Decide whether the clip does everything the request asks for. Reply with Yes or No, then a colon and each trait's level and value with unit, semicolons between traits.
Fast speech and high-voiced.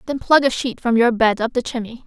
Yes: fast, 290 wpm; high, 240 Hz